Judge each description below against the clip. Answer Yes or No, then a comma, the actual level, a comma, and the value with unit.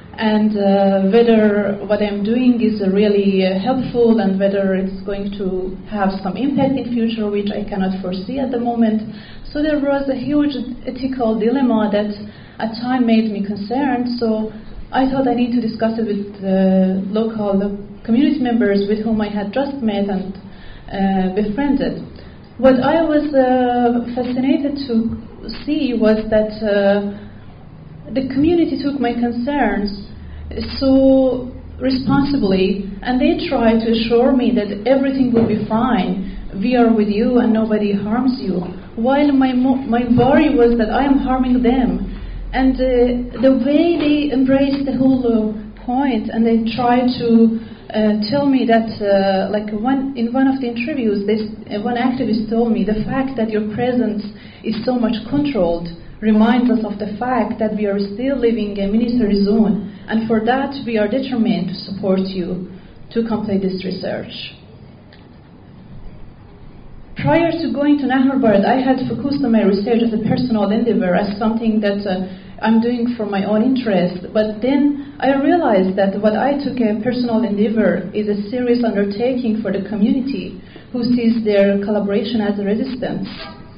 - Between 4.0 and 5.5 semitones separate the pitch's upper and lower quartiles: No, average, 3.6 semitones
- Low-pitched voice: No, high, 225 Hz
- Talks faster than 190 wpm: No, average, 165 wpm